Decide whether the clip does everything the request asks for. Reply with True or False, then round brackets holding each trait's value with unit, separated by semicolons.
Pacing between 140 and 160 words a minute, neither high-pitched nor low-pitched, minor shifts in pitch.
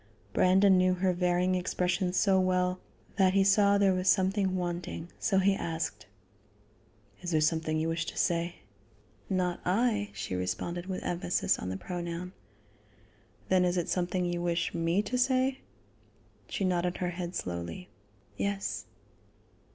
True (145 wpm; 180 Hz; 1.8 semitones)